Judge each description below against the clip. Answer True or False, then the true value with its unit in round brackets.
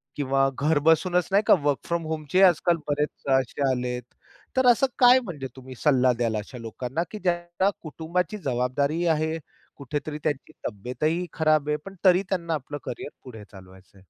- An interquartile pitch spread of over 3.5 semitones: True (5.0 semitones)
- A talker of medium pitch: True (150 Hz)